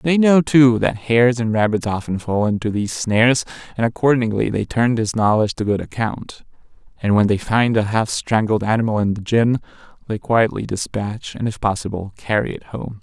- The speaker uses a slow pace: No, average, 190 wpm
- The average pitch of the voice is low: Yes, low, 110 Hz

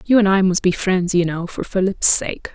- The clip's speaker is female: Yes, female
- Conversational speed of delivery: No, fast, 260 wpm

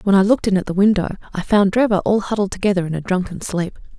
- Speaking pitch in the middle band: No, high, 195 Hz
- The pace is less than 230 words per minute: No, fast, 255 wpm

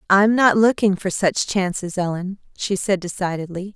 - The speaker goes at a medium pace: Yes, average, 160 wpm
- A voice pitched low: No, high, 190 Hz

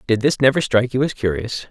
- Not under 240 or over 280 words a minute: Yes, fast, 245 wpm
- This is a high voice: No, low, 120 Hz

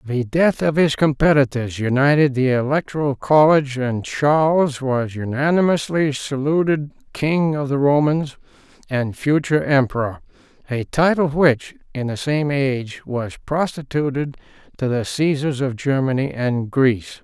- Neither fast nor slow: No, slow, 130 wpm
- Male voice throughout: Yes, male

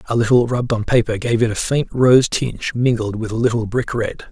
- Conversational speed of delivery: No, fast, 235 wpm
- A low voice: Yes, low, 115 Hz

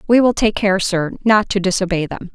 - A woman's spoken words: Yes, female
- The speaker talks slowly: No, fast, 230 wpm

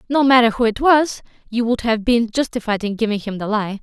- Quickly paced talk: Yes, fast, 235 wpm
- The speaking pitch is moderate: No, high, 230 Hz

